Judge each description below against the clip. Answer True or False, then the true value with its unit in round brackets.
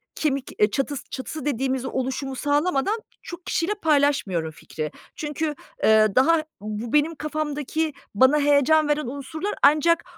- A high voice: True (285 Hz)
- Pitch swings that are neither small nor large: True (3.0 semitones)